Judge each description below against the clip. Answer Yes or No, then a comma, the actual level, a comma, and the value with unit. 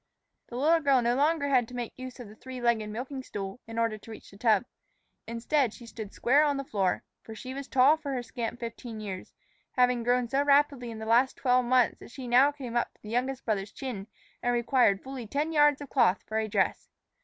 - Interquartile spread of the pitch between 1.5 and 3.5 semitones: Yes, average, 3.1 semitones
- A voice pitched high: Yes, high, 245 Hz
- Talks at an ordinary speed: No, fast, 230 wpm